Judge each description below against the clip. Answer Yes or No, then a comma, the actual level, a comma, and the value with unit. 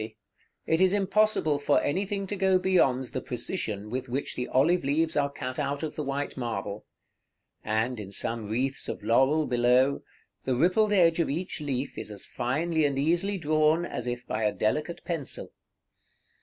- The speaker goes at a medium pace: Yes, average, 175 wpm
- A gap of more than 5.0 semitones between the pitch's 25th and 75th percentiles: Yes, wide, 5.4 semitones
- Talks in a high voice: No, medium, 140 Hz